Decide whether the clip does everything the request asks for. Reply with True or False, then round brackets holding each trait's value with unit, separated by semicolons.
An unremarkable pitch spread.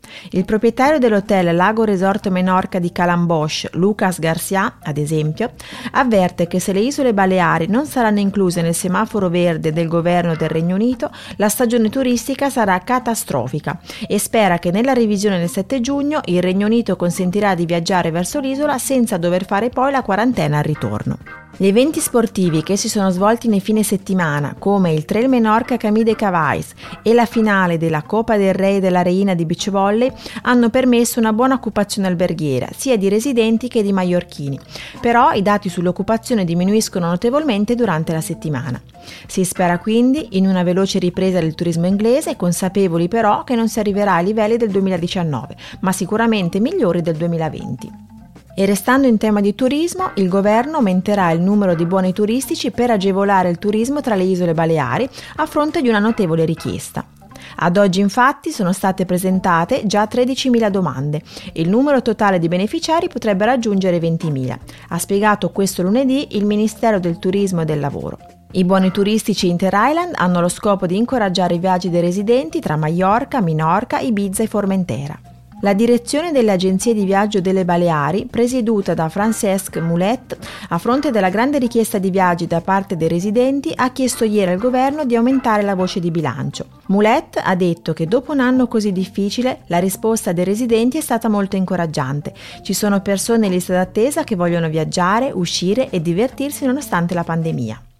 True (4.7 semitones)